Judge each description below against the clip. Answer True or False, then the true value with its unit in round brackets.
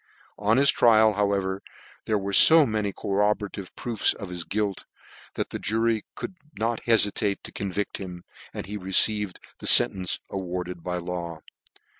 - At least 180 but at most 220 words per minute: False (150 wpm)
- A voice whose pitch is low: True (100 Hz)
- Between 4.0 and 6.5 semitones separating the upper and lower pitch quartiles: False (2.8 semitones)